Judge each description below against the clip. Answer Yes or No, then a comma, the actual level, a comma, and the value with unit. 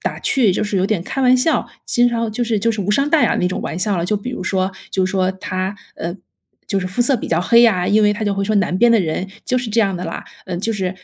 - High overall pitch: Yes, high, 205 Hz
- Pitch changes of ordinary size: Yes, average, 3.8 semitones